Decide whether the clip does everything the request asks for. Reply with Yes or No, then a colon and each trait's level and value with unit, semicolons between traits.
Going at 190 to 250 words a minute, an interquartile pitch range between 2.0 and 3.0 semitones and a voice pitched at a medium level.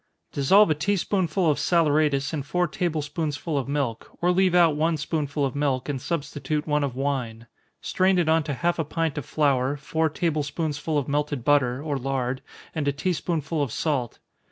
Yes: average, 200 wpm; average, 2.7 semitones; medium, 150 Hz